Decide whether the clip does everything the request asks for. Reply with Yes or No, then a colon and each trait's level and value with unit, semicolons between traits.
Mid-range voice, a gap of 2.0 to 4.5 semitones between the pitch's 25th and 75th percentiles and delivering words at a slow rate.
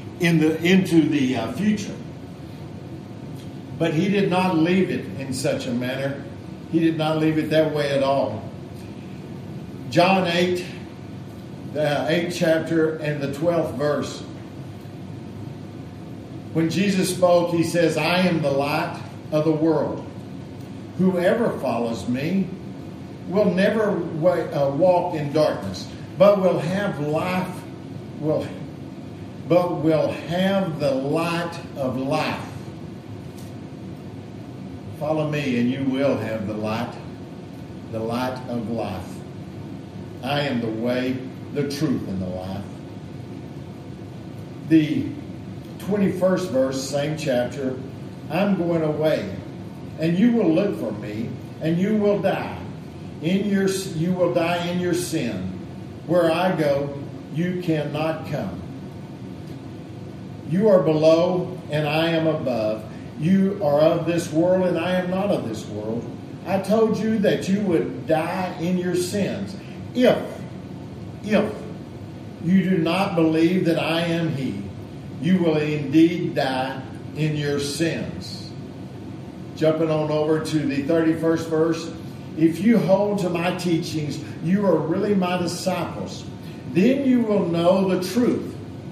Yes: medium, 160 Hz; average, 4.2 semitones; slow, 130 wpm